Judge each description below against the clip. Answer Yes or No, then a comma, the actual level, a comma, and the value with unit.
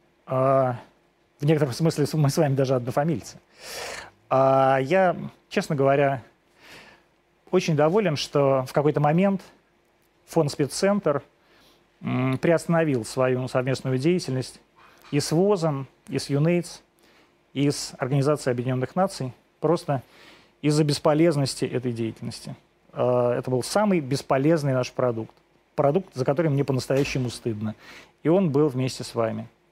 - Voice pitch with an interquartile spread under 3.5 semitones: No, average, 4.0 semitones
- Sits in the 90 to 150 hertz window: Yes, medium, 140 Hz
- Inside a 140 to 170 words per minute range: No, average, 115 wpm